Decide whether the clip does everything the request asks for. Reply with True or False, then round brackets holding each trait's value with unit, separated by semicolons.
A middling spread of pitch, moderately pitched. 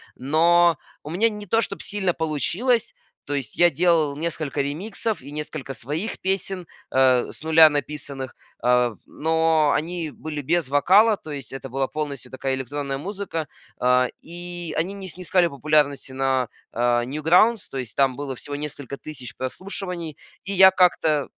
True (4.5 semitones; 155 Hz)